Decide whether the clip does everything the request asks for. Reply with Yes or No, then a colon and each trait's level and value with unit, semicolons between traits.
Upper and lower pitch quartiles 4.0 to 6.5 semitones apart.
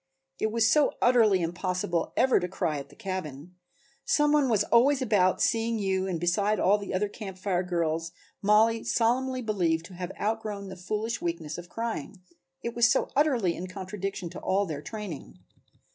Yes: average, 4.3 semitones